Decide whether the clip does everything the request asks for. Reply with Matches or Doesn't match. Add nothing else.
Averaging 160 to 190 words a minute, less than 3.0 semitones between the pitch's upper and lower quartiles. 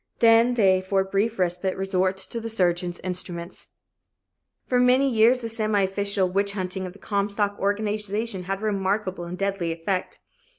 Matches